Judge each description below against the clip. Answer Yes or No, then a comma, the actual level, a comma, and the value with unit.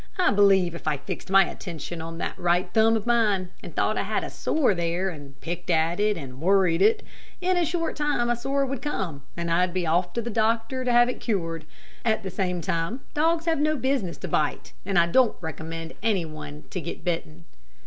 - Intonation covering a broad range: Yes, wide, 6.1 semitones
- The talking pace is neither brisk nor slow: No, fast, 220 wpm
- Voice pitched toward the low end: No, high, 190 Hz